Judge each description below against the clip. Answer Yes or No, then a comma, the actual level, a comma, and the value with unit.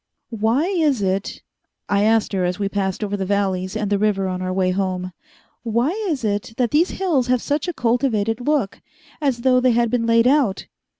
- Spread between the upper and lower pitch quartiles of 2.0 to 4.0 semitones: No, average, 4.4 semitones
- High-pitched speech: Yes, high, 220 Hz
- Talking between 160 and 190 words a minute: No, average, 200 wpm